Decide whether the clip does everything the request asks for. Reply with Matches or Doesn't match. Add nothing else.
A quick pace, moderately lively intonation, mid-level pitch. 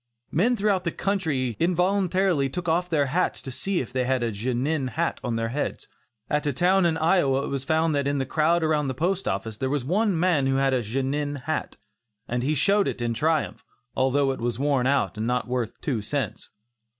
Matches